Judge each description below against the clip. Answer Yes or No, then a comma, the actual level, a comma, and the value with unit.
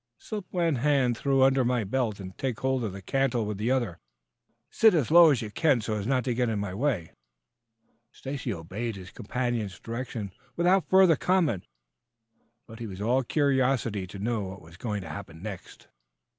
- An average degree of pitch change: Yes, average, 4.8 semitones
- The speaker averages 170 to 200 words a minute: Yes, average, 185 wpm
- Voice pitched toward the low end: Yes, low, 120 Hz